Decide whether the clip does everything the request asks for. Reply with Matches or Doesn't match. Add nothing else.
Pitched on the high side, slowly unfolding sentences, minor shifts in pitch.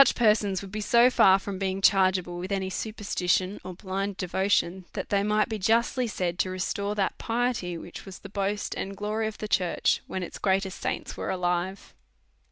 Doesn't match